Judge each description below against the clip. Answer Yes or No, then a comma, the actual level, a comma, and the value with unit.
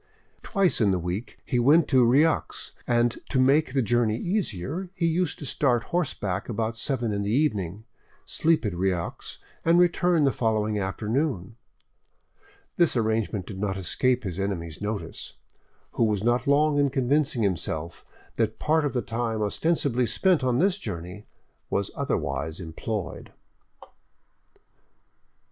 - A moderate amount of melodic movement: No, wide, 6.2 semitones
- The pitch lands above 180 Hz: No, low, 120 Hz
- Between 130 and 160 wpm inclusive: Yes, average, 140 wpm